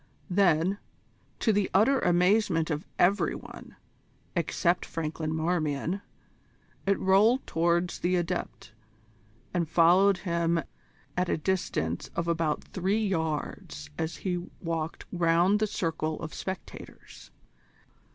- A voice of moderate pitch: Yes, medium, 175 Hz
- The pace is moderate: No, slow, 110 wpm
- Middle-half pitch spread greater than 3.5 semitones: No, average, 2.8 semitones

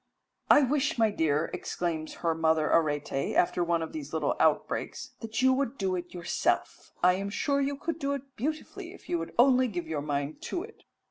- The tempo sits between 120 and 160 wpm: No, average, 200 wpm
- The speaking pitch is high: Yes, high, 195 Hz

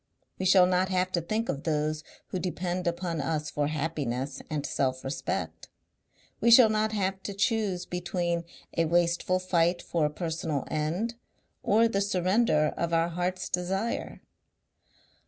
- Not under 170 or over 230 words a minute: No, average, 145 wpm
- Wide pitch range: No, average, 3.4 semitones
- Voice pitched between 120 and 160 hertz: No, medium, 175 Hz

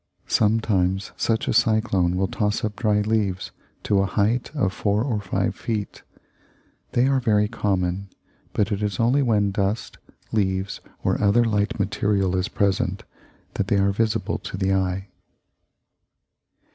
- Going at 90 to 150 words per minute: Yes, average, 145 wpm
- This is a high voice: No, low, 105 Hz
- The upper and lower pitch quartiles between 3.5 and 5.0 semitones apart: No, narrow, 2.4 semitones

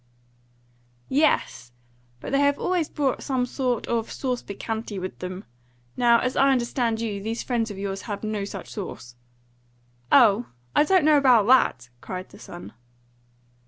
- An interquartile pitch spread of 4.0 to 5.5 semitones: Yes, average, 4.7 semitones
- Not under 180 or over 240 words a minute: No, average, 155 wpm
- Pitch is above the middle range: Yes, high, 235 Hz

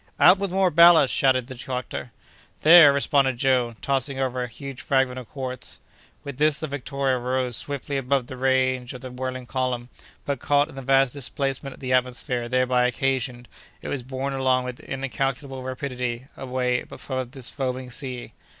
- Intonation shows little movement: Yes, narrow, 1.5 semitones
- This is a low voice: Yes, low, 130 Hz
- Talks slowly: No, average, 170 wpm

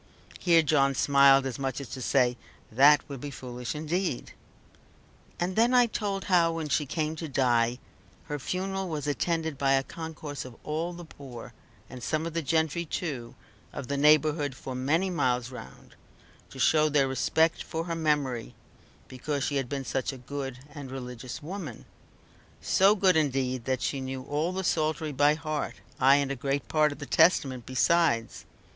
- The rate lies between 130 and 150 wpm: No, average, 175 wpm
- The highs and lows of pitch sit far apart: No, average, 3.6 semitones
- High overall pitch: No, medium, 145 Hz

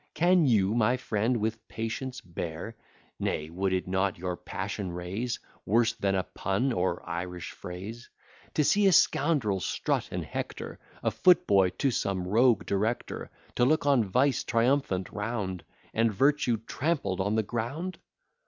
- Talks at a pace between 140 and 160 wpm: Yes, average, 155 wpm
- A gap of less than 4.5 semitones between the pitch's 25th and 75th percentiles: No, average, 5.1 semitones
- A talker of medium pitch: No, low, 110 Hz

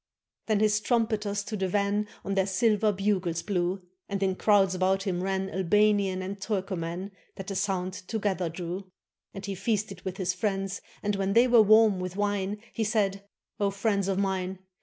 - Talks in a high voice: Yes, high, 195 Hz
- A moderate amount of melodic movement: No, narrow, 1.8 semitones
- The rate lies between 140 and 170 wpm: No, average, 180 wpm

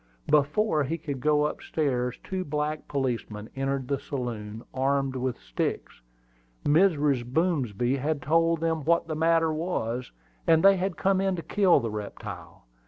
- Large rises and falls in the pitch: No, average, 4.5 semitones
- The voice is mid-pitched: Yes, medium, 150 Hz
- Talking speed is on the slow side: No, average, 155 wpm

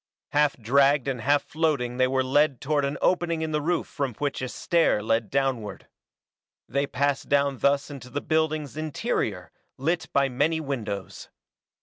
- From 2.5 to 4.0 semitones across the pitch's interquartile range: Yes, average, 2.9 semitones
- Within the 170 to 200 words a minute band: No, average, 160 wpm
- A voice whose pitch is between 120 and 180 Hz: Yes, medium, 140 Hz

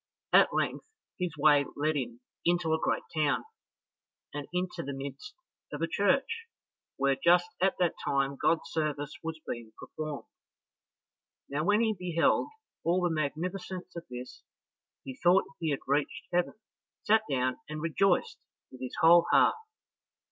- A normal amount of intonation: Yes, average, 3.9 semitones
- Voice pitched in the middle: Yes, medium, 160 Hz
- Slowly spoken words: No, average, 150 wpm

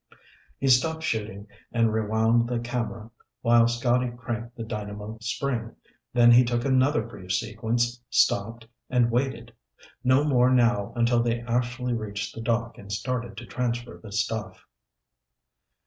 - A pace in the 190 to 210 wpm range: No, average, 140 wpm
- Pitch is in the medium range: No, low, 120 Hz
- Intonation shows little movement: Yes, narrow, 1.7 semitones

